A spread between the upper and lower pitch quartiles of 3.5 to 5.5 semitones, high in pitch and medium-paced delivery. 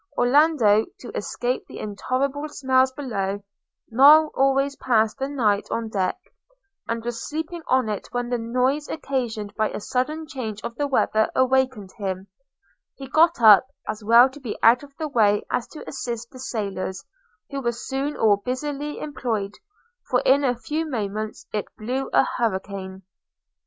Yes: average, 4.2 semitones; high, 245 Hz; average, 160 wpm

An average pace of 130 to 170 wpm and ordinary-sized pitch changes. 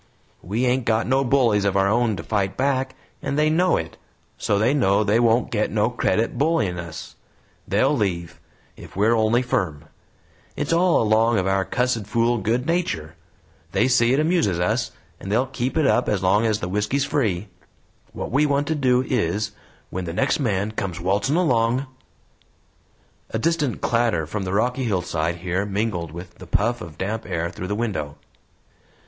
No: average, 180 wpm; average, 5.0 semitones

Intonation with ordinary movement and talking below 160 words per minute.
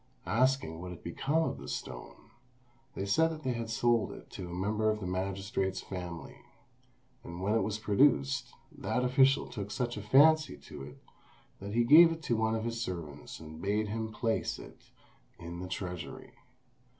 No: average, 4.9 semitones; average, 175 wpm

